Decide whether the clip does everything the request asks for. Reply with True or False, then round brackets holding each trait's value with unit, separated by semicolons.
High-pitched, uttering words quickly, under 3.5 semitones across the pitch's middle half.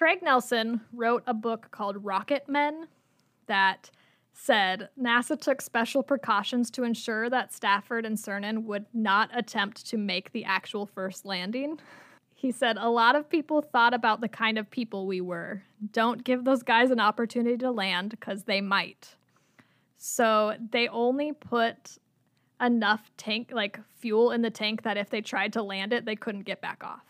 False (230 Hz; 170 wpm; 3.1 semitones)